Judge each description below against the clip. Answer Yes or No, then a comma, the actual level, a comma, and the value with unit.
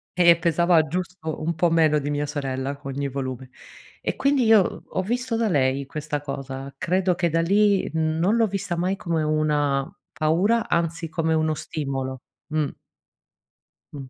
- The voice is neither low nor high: Yes, medium, 160 Hz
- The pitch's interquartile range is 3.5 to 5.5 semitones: Yes, average, 4.1 semitones